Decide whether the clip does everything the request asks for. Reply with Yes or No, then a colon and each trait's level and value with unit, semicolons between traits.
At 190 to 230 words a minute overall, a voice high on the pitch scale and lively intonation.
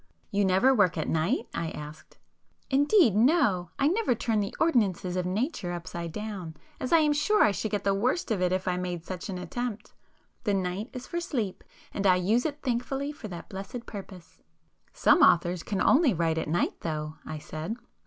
Yes: average, 195 wpm; high, 200 Hz; wide, 6.1 semitones